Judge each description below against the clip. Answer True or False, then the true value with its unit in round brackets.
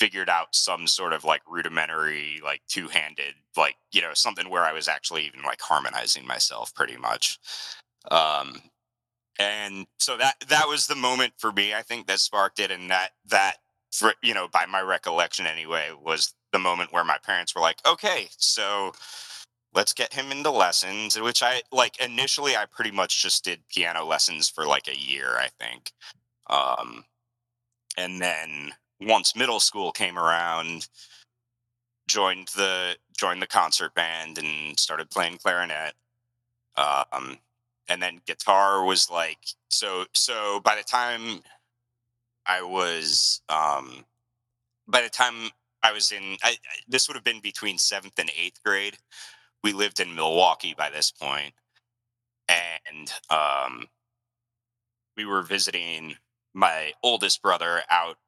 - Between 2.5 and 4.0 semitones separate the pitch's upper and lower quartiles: False (4.9 semitones)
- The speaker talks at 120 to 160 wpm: True (150 wpm)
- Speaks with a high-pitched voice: False (110 Hz)